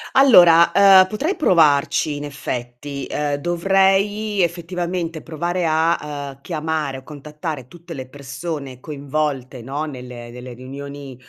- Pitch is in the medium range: Yes, medium, 150 Hz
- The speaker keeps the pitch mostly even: No, average, 3.9 semitones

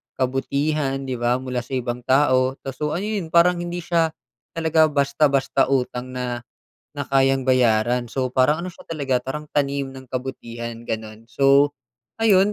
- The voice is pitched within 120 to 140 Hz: Yes, low, 135 Hz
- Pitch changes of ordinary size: Yes, average, 3.1 semitones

